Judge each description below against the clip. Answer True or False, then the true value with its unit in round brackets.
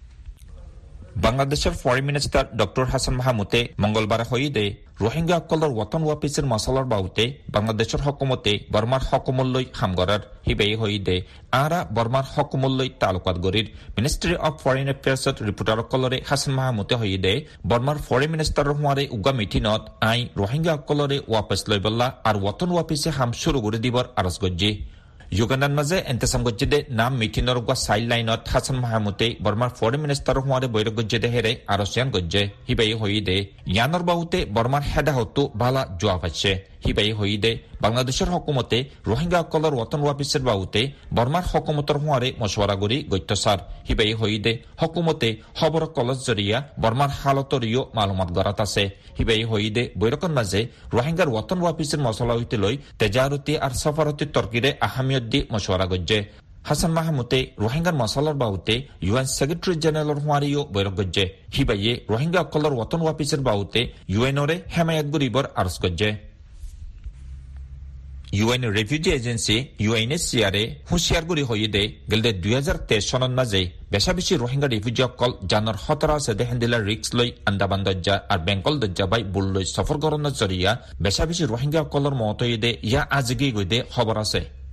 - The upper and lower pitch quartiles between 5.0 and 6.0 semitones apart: True (5.3 semitones)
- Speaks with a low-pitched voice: True (120 Hz)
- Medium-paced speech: False (125 wpm)